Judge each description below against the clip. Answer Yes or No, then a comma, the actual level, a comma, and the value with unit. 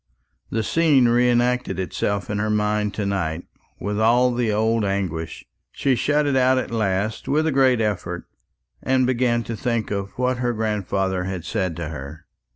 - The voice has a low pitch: Yes, low, 110 Hz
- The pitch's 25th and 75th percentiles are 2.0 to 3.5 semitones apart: No, average, 4.2 semitones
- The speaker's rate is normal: Yes, average, 175 wpm